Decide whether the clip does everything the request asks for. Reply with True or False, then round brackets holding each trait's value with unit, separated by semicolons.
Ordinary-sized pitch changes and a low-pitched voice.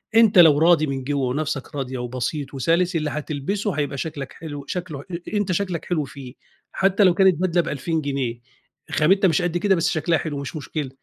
False (4.1 semitones; 155 Hz)